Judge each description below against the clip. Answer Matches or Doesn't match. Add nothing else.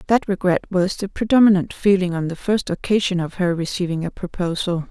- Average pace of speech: Matches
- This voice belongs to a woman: Matches